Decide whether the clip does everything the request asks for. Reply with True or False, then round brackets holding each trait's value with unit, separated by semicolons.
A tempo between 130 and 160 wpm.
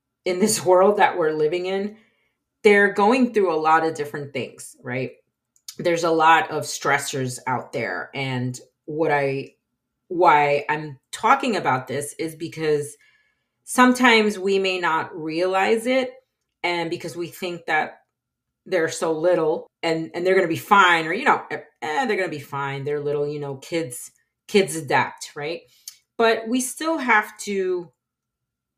True (155 wpm)